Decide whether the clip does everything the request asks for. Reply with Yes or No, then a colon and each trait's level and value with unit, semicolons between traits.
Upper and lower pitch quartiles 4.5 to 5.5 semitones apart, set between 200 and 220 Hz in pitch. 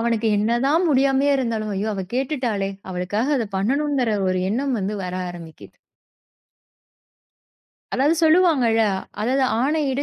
No: average, 4.8 semitones; high, 245 Hz